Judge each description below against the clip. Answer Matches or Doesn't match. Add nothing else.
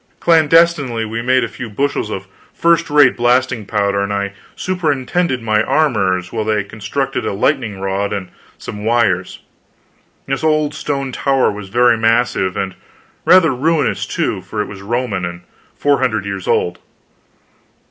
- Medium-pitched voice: Doesn't match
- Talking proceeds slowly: Doesn't match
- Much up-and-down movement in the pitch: Matches